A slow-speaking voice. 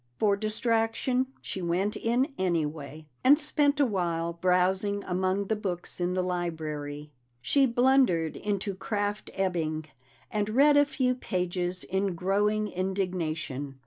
Yes: slow, 130 wpm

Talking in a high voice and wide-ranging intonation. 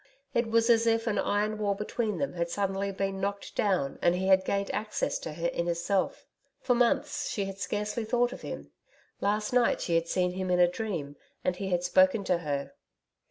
No: high, 195 Hz; average, 3.6 semitones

